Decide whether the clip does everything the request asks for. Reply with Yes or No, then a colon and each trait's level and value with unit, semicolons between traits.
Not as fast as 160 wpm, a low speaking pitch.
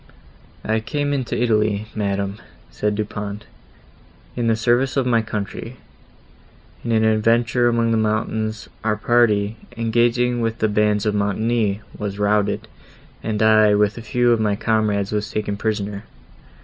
Yes: average, 150 wpm; low, 110 Hz